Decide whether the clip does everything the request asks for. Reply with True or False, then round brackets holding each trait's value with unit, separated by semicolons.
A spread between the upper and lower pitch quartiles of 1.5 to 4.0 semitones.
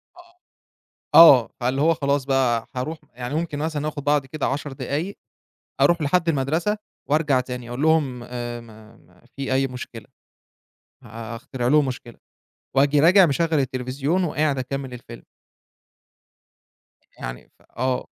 True (3.7 semitones)